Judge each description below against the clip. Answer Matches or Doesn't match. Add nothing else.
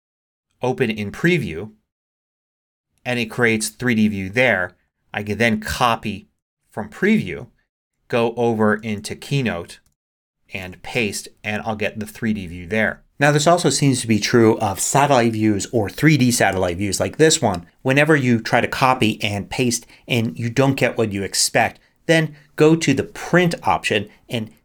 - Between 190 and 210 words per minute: Doesn't match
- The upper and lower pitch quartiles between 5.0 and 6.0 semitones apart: Doesn't match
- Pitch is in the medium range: Doesn't match